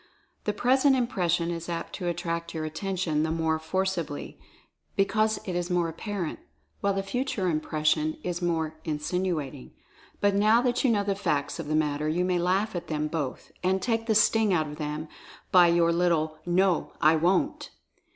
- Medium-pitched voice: Yes, medium, 175 Hz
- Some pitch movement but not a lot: Yes, average, 3.8 semitones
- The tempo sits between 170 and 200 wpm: Yes, average, 185 wpm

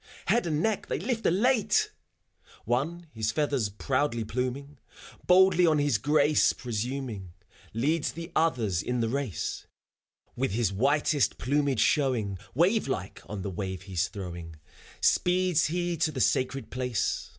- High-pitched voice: No, low, 135 Hz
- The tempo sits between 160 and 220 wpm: No, average, 140 wpm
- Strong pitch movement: Yes, wide, 6.7 semitones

